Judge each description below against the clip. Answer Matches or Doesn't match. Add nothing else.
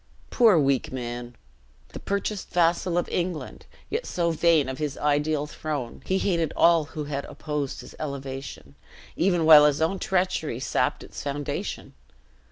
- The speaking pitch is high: Doesn't match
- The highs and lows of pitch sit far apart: Doesn't match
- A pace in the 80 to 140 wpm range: Doesn't match